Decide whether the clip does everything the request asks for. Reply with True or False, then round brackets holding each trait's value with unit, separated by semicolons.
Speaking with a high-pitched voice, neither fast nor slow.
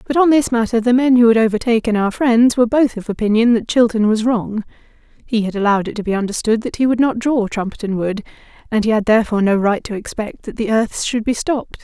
False (225 Hz; 240 wpm)